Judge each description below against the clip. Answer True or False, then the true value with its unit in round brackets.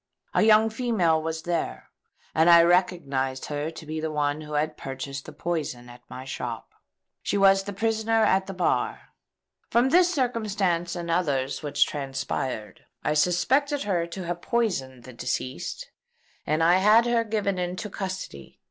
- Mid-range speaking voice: True (170 Hz)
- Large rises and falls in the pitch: True (6.0 semitones)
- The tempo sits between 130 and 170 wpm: True (160 wpm)